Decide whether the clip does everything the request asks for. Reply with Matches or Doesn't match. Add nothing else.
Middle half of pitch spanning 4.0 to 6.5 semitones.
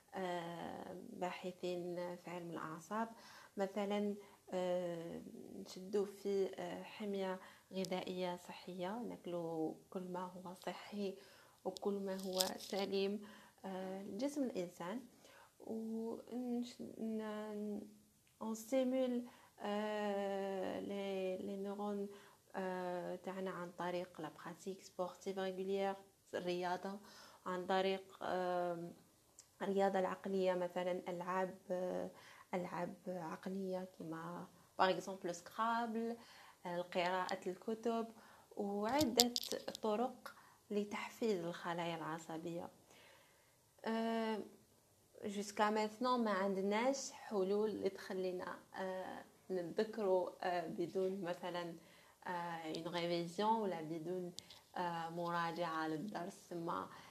Doesn't match